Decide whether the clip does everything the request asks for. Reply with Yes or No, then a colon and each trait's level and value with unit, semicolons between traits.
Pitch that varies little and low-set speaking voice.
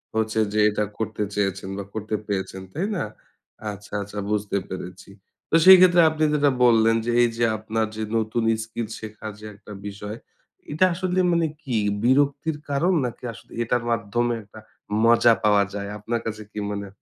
No: average, 3.0 semitones; low, 110 Hz